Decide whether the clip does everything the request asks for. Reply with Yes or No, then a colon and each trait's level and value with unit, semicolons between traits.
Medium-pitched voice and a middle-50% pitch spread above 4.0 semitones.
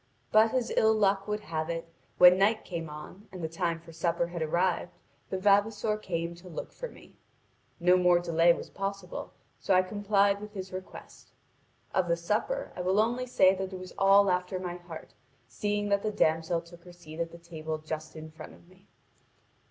No: medium, 180 Hz; average, 3.0 semitones